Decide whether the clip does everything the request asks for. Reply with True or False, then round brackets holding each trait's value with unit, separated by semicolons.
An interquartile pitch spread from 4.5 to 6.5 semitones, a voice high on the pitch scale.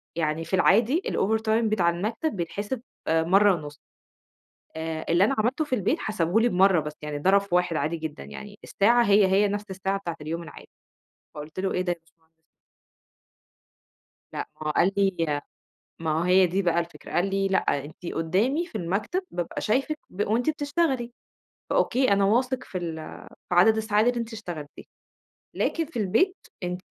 True (4.8 semitones; 195 Hz)